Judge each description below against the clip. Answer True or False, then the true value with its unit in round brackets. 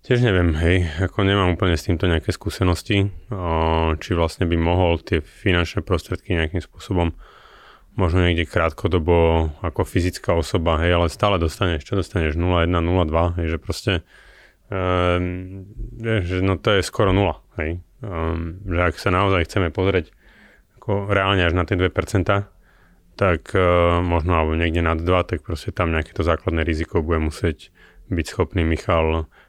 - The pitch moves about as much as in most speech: False (2.3 semitones)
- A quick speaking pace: False (155 wpm)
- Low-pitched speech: True (90 Hz)